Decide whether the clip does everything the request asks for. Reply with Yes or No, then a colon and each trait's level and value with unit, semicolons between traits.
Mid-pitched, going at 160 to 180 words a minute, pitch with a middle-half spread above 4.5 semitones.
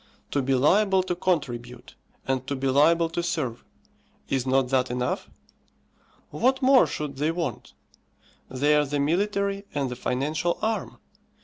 No: medium, 145 Hz; average, 145 wpm; average, 5.1 semitones